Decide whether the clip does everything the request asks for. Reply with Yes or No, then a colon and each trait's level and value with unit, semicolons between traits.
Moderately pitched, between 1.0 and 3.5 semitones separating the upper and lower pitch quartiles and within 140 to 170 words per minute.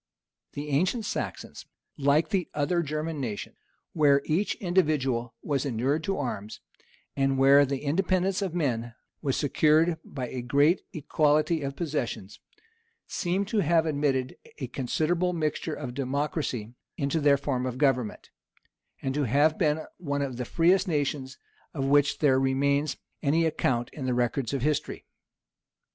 Yes: medium, 145 Hz; average, 3.2 semitones; average, 145 wpm